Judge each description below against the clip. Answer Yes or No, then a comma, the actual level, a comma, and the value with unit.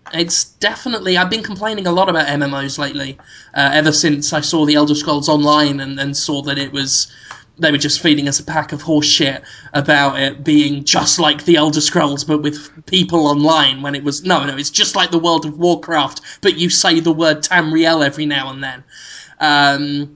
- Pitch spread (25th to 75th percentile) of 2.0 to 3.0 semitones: Yes, narrow, 2.5 semitones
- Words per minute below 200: No, fast, 205 wpm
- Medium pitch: Yes, medium, 150 Hz